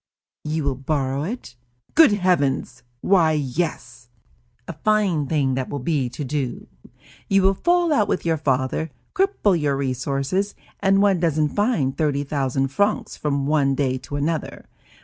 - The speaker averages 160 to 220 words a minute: No, average, 150 wpm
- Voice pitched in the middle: Yes, medium, 150 Hz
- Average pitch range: No, wide, 5.8 semitones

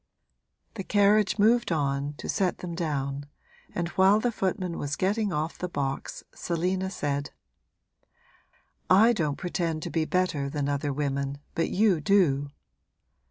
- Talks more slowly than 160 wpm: Yes, average, 140 wpm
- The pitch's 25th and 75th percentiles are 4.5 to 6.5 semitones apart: Yes, average, 4.9 semitones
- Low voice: No, medium, 170 Hz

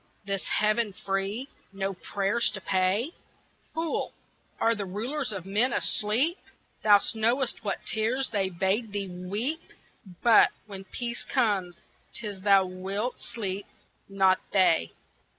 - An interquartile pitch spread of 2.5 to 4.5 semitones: Yes, average, 3.4 semitones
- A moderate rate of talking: No, slow, 125 wpm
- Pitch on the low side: No, high, 205 Hz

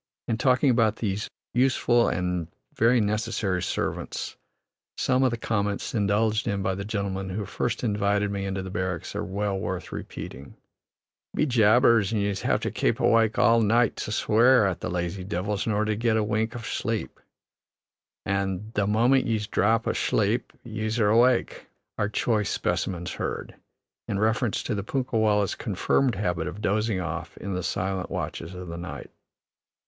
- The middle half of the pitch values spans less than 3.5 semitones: Yes, average, 2.8 semitones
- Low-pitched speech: Yes, low, 105 Hz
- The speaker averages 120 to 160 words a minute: No, average, 170 wpm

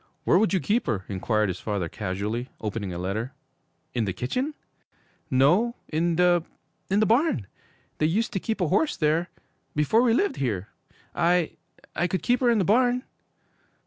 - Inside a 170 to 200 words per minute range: Yes, average, 175 wpm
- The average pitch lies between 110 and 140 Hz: No, medium, 170 Hz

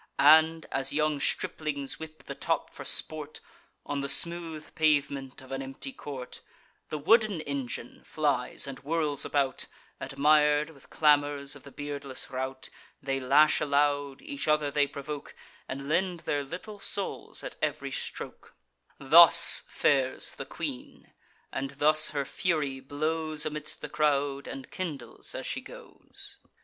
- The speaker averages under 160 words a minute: Yes, average, 140 wpm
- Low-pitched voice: No, medium, 145 Hz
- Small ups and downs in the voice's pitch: Yes, narrow, 2.1 semitones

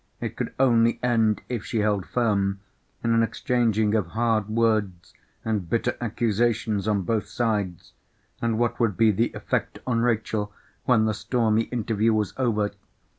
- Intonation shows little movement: Yes, narrow, 1.9 semitones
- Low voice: Yes, low, 110 Hz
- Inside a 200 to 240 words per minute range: No, average, 155 wpm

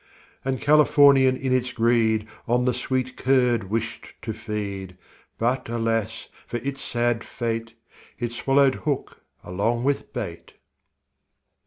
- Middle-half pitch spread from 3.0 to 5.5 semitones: No, narrow, 2.5 semitones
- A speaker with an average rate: No, slow, 125 wpm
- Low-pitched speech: Yes, low, 120 Hz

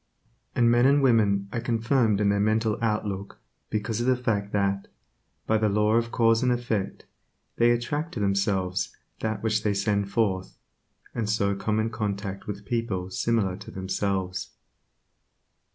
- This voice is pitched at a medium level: No, low, 105 Hz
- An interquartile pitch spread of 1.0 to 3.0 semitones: Yes, average, 2.7 semitones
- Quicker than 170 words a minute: No, average, 155 wpm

